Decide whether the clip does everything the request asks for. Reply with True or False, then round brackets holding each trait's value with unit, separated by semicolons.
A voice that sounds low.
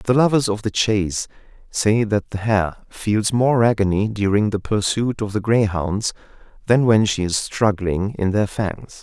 True (105 Hz)